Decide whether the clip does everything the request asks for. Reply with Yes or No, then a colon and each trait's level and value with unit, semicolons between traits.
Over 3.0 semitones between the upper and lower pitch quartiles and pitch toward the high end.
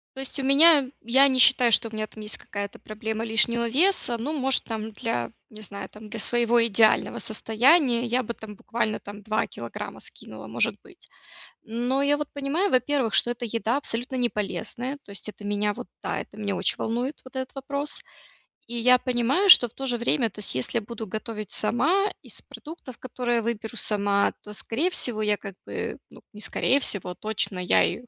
Yes: average, 3.5 semitones; high, 235 Hz